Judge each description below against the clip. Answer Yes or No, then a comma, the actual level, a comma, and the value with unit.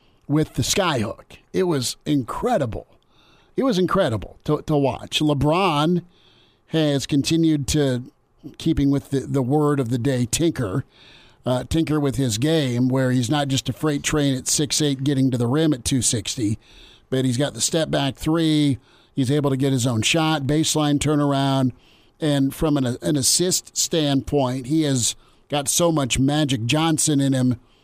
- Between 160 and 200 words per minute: Yes, average, 165 wpm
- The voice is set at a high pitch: No, medium, 140 Hz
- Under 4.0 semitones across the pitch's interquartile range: Yes, average, 3.0 semitones